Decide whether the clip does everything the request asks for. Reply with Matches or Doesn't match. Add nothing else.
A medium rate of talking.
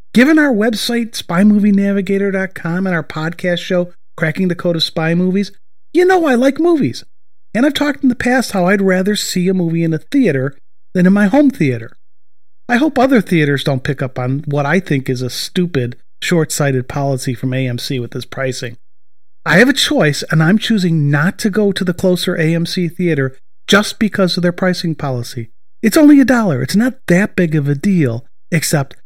Matches